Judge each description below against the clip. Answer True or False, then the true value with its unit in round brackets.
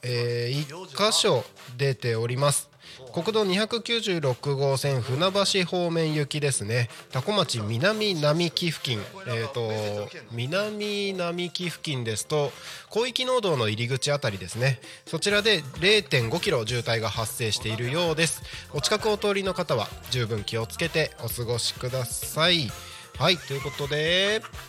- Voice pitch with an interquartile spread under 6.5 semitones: False (6.9 semitones)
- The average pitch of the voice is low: False (145 Hz)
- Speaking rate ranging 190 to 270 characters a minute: True (265 characters per minute)